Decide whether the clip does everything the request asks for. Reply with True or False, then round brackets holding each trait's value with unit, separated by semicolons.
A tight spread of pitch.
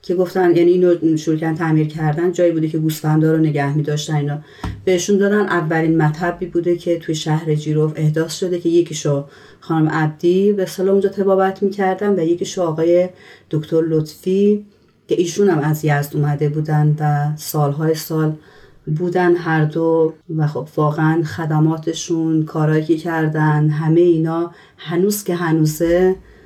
True (2.3 semitones)